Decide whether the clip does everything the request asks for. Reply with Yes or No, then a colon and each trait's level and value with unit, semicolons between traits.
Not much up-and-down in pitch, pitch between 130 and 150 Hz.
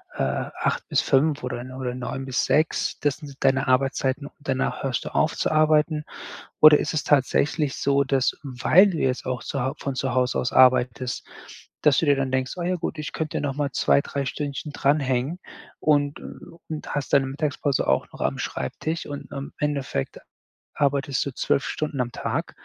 Yes: narrow, 2.3 semitones; medium, 140 Hz